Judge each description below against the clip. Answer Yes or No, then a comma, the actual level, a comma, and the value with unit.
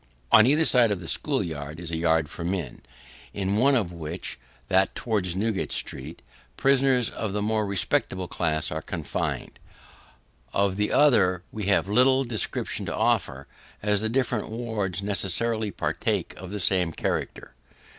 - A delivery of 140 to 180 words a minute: Yes, average, 155 wpm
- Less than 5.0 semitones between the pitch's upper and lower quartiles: Yes, average, 4.4 semitones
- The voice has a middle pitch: No, low, 100 Hz